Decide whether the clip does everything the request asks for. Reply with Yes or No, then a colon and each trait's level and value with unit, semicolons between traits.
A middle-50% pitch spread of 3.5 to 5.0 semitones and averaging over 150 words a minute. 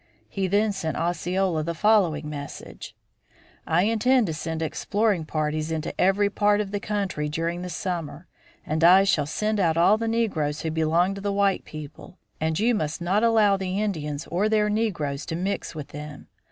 Yes: average, 4.7 semitones; average, 180 wpm